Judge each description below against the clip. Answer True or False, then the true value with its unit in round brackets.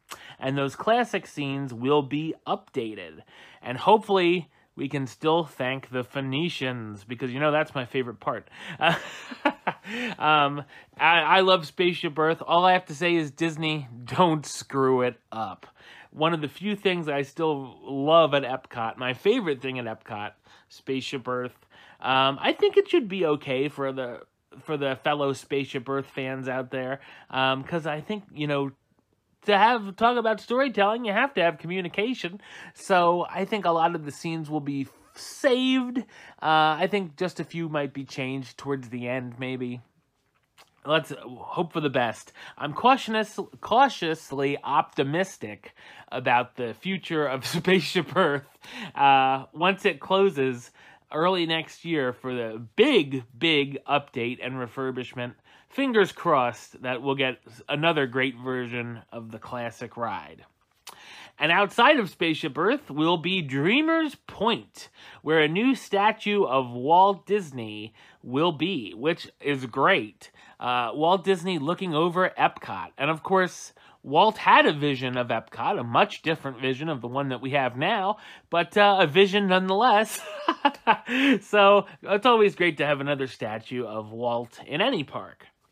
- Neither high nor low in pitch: True (150 Hz)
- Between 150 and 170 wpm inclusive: True (155 wpm)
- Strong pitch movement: True (5.9 semitones)